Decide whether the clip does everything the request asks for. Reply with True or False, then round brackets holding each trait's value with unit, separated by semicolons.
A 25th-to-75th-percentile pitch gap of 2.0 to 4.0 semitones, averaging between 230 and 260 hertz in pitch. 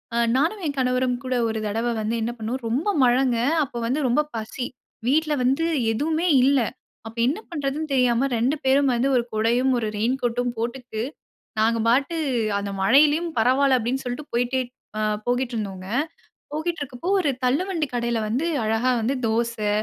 True (3.2 semitones; 250 Hz)